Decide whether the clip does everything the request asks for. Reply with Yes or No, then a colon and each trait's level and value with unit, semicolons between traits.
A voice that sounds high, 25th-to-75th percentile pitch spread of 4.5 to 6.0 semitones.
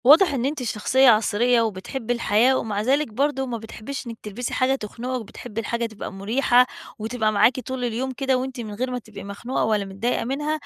No: high, 240 Hz; average, 3.3 semitones